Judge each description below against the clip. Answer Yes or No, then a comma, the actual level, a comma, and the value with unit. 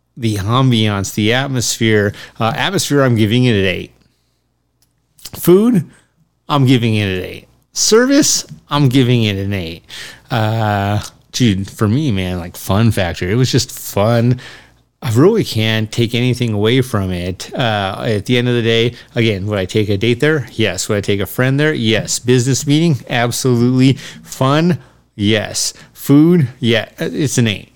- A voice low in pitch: Yes, low, 115 Hz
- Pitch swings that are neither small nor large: Yes, average, 4.2 semitones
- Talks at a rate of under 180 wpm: Yes, average, 160 wpm